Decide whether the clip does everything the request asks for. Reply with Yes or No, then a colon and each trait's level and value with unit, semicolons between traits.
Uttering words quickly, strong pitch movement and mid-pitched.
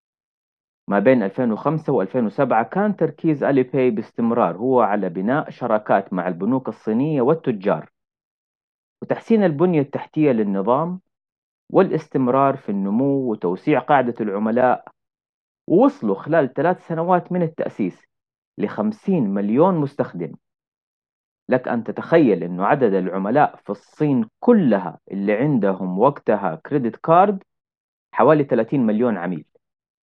No: average, 110 wpm; wide, 7.6 semitones; medium, 145 Hz